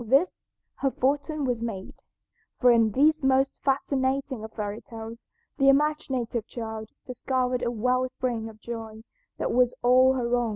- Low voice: No, very high, 250 Hz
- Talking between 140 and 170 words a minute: Yes, average, 160 wpm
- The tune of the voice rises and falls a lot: No, average, 2.9 semitones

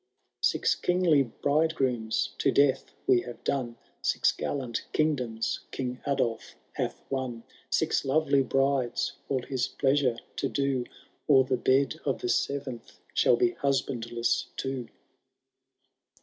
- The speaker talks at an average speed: No, slow, 120 wpm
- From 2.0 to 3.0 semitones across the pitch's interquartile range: Yes, narrow, 2.4 semitones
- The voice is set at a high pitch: No, low, 135 Hz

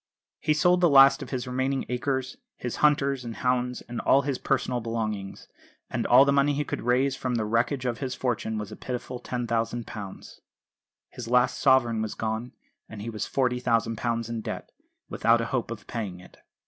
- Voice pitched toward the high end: No, low, 125 Hz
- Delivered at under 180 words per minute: No, average, 185 wpm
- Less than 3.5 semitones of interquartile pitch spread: Yes, narrow, 2.5 semitones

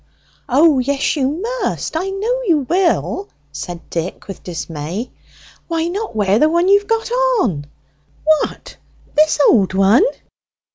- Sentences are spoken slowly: Yes, slow, 130 wpm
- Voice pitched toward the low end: No, very high, 305 Hz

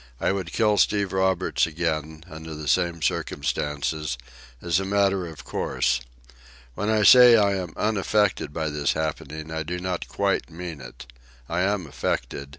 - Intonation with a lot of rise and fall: No, average, 4.0 semitones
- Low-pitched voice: Yes, very low, 85 Hz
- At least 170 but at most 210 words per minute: No, average, 155 wpm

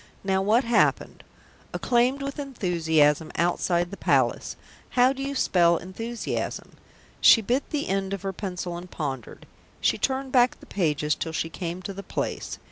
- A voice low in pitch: No, high, 195 Hz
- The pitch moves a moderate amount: No, wide, 6.2 semitones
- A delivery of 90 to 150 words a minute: No, average, 160 wpm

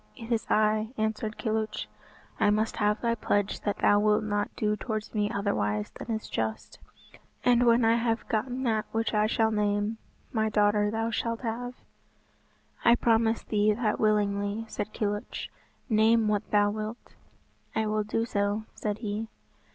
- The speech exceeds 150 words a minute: Yes, average, 160 wpm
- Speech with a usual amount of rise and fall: No, narrow, 1.4 semitones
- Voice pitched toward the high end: Yes, high, 215 Hz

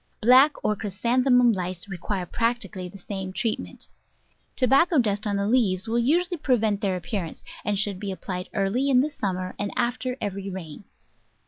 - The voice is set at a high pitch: Yes, high, 210 Hz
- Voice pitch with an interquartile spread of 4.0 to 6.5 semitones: Yes, average, 4.6 semitones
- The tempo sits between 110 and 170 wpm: Yes, average, 165 wpm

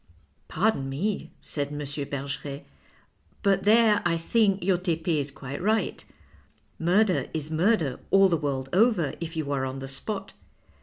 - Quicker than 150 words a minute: Yes, average, 160 wpm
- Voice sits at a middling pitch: Yes, medium, 165 Hz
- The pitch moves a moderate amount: No, wide, 5.7 semitones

